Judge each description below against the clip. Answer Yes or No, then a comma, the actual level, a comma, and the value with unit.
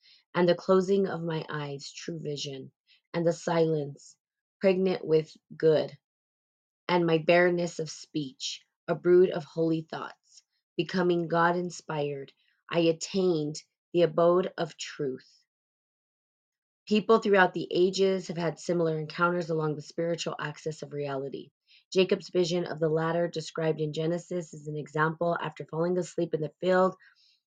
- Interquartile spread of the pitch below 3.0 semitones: Yes, narrow, 2.4 semitones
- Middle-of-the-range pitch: Yes, medium, 170 Hz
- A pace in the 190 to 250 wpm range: No, average, 140 wpm